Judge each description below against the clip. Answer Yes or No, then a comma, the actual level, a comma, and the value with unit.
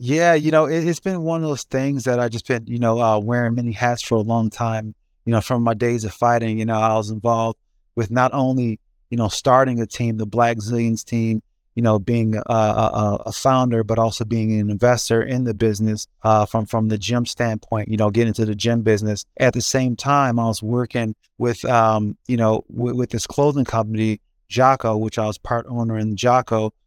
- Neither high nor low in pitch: No, low, 115 Hz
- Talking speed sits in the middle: No, fast, 225 wpm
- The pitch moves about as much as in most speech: No, narrow, 1.9 semitones